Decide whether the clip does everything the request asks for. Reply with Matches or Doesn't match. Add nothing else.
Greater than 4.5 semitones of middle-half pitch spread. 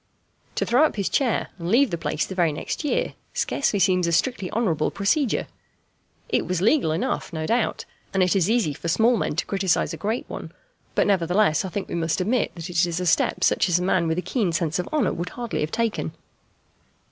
Matches